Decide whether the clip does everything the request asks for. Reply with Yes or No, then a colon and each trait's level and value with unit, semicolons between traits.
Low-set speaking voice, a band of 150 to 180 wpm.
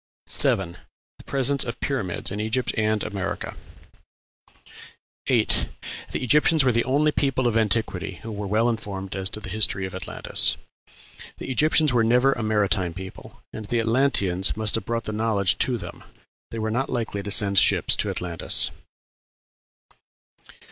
Yes: low, 110 Hz; average, 155 wpm